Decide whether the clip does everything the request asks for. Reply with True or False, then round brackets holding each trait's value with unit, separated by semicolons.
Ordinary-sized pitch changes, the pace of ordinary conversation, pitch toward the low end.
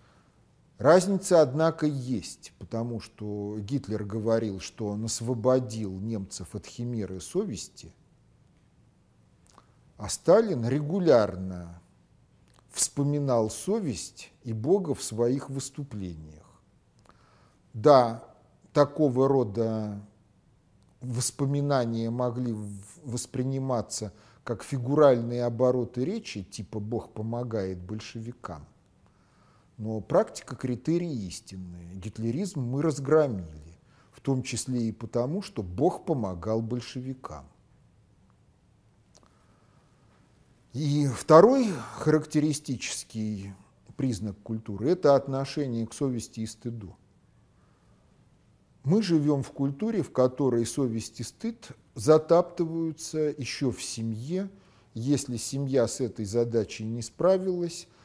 False (4.5 semitones; 90 wpm; 120 Hz)